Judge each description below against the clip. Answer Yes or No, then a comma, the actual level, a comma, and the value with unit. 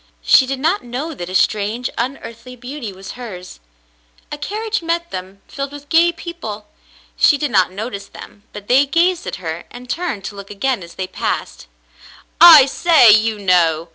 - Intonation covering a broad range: Yes, wide, 7.0 semitones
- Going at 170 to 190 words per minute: Yes, average, 175 wpm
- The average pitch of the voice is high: Yes, high, 245 Hz